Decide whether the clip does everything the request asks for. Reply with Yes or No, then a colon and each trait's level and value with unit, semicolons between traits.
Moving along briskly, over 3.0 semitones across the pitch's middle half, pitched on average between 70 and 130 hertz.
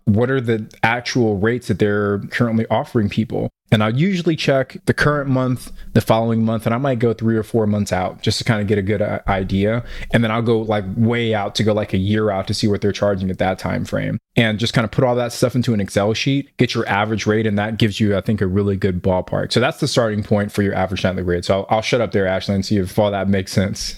No: fast, 275 wpm; narrow, 2.5 semitones; low, 110 Hz